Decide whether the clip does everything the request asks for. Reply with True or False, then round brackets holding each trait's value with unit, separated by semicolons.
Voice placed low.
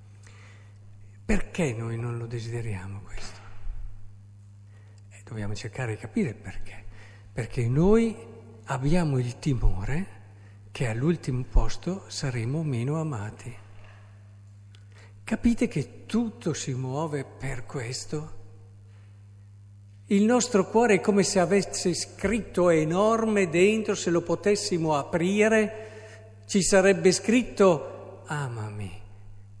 True (120 Hz)